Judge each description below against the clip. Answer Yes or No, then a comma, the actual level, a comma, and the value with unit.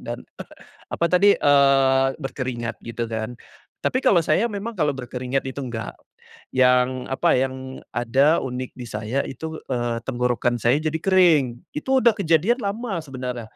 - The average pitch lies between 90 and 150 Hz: Yes, low, 135 Hz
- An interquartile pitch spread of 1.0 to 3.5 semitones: No, average, 4.6 semitones